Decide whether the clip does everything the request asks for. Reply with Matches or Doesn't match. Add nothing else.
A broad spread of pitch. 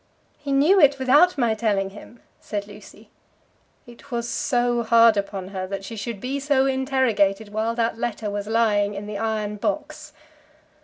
Doesn't match